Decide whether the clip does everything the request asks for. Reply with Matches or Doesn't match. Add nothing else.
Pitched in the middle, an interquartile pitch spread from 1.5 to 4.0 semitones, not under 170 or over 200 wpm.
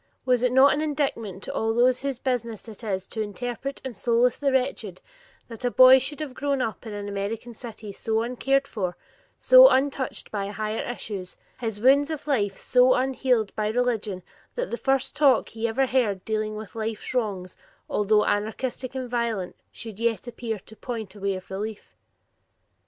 Doesn't match